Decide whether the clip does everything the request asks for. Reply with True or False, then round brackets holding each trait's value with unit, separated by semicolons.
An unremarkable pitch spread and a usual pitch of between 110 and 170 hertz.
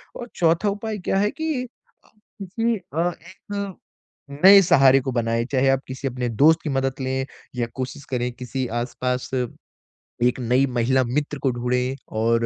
False (5.9 semitones; 135 Hz)